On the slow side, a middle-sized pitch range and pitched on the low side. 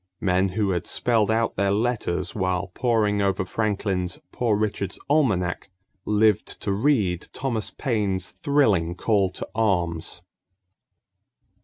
Yes: slow, 120 wpm; average, 3.3 semitones; low, 100 Hz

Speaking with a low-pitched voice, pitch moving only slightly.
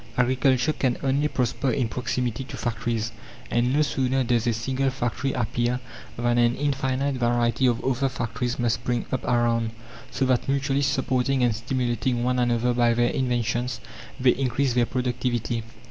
Yes: low, 125 Hz; narrow, 1.8 semitones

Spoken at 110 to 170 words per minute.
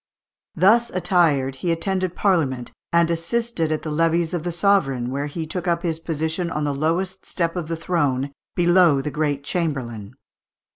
Yes: average, 165 wpm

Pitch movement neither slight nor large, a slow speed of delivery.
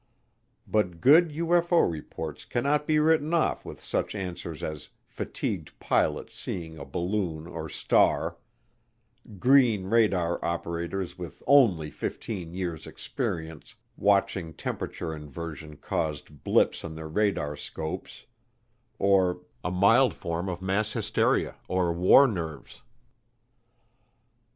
Yes: average, 5.0 semitones; slow, 110 wpm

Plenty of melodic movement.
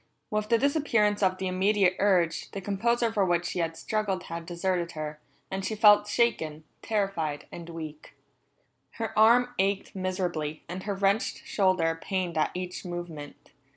No: average, 3.6 semitones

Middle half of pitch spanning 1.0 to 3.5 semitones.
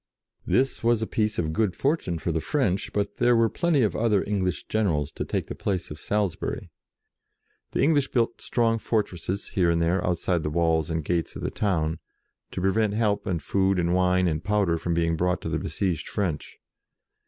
No: average, 4.5 semitones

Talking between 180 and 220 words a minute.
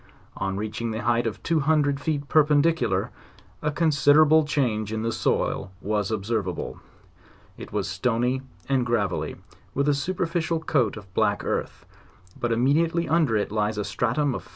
No: average, 155 wpm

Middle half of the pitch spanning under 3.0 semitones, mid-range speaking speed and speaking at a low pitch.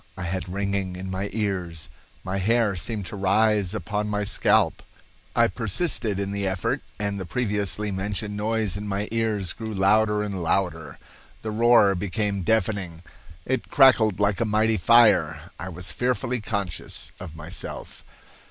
Yes: narrow, 2.6 semitones; average, 150 wpm; low, 100 Hz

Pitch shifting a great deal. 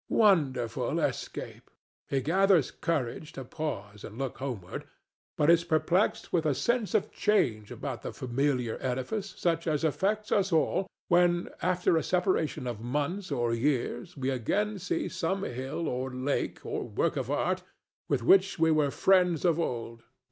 Yes: wide, 6.1 semitones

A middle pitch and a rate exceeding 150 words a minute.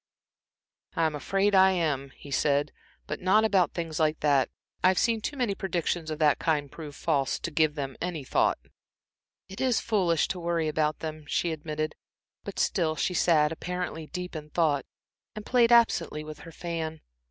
Yes: medium, 160 Hz; average, 175 wpm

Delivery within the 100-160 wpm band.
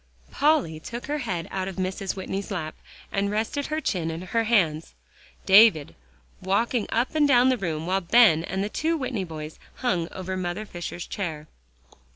No: average, 175 wpm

